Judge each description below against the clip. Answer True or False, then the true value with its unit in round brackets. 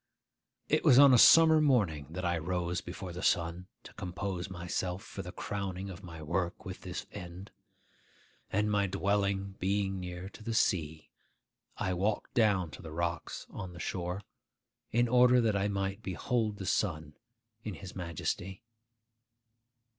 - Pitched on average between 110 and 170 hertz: False (95 Hz)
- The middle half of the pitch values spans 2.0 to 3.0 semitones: True (2.7 semitones)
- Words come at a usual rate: True (155 wpm)